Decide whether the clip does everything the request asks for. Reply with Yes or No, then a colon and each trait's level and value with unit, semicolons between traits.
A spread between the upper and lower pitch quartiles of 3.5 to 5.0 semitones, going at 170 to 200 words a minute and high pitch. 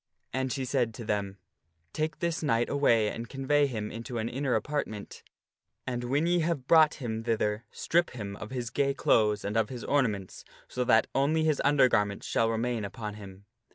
No: average, 4.7 semitones; average, 190 wpm; low, 120 Hz